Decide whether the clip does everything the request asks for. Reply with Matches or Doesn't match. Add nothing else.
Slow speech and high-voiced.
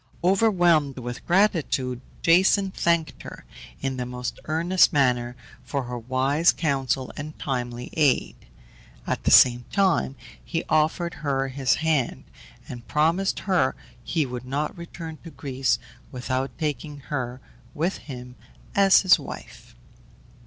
Doesn't match